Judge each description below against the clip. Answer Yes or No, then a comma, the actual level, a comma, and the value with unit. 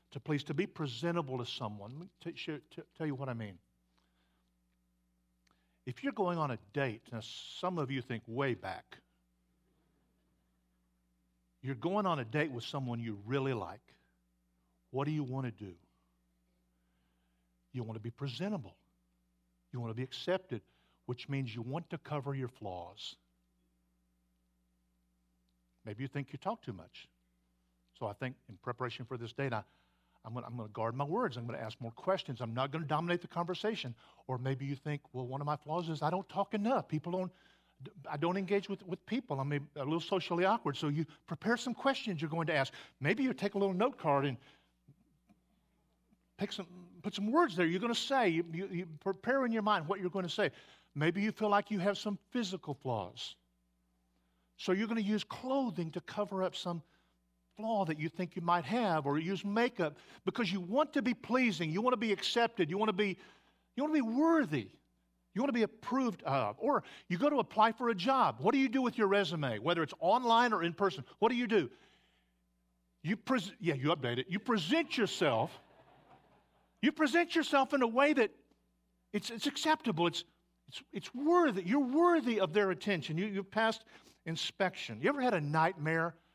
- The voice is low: No, medium, 155 Hz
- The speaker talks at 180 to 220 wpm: Yes, average, 190 wpm